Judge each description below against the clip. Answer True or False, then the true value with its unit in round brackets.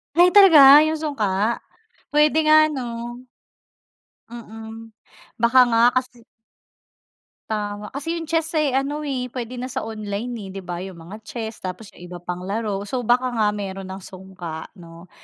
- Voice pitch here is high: True (230 Hz)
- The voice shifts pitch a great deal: True (5.8 semitones)